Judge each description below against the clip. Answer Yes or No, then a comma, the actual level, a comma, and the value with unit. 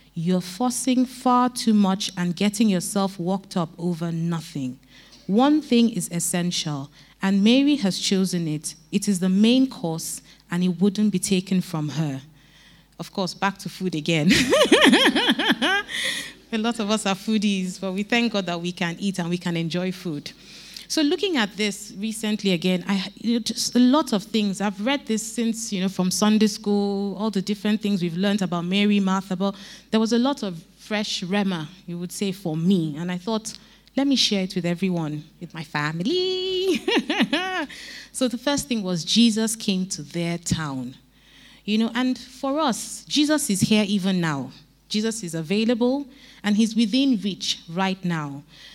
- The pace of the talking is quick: No, average, 175 wpm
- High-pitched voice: Yes, high, 200 Hz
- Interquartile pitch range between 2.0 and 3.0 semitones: No, average, 4.4 semitones